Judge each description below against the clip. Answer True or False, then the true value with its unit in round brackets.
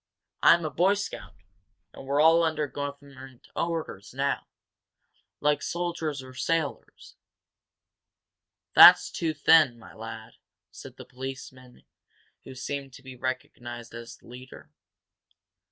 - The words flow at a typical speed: False (120 wpm)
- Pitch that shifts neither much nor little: True (3.6 semitones)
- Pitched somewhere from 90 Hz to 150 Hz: True (135 Hz)